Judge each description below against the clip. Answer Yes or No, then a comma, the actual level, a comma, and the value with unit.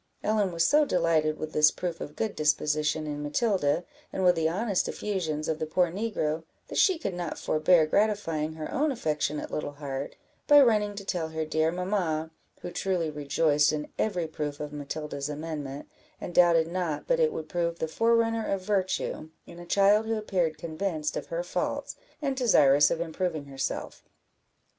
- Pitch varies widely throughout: No, average, 4.5 semitones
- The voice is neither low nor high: Yes, medium, 165 Hz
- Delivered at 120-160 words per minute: No, average, 175 wpm